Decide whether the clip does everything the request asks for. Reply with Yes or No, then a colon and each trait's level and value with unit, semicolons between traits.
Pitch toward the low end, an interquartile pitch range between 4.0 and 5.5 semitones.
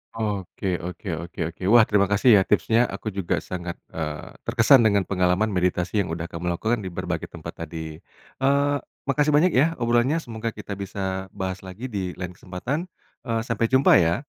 Yes: low, 100 Hz; average, 4.7 semitones